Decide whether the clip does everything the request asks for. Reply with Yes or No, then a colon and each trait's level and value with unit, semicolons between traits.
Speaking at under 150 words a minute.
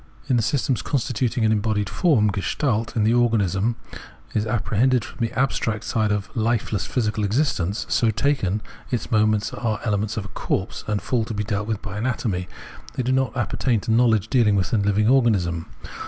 No: average, 180 wpm